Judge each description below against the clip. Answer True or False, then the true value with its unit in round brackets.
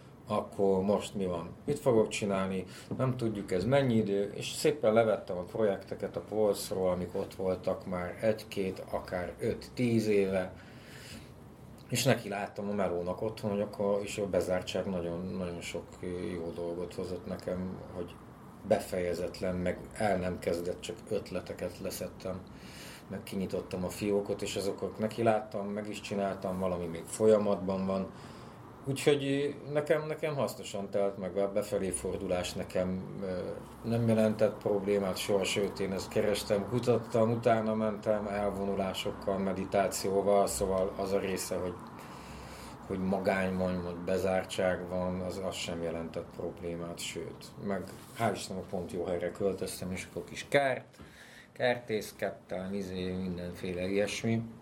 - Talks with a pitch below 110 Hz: True (100 Hz)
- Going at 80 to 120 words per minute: False (135 wpm)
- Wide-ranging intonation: False (2.7 semitones)